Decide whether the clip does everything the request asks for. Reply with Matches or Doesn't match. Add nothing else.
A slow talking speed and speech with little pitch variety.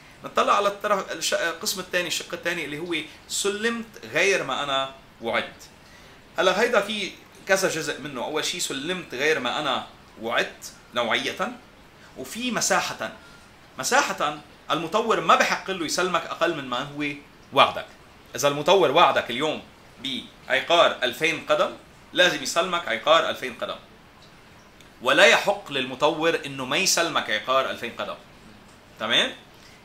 Doesn't match